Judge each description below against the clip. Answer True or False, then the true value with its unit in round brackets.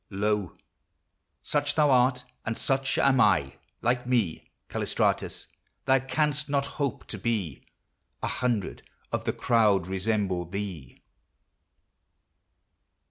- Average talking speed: False (110 wpm)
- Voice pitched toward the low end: True (115 Hz)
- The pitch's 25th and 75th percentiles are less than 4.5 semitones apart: False (5.5 semitones)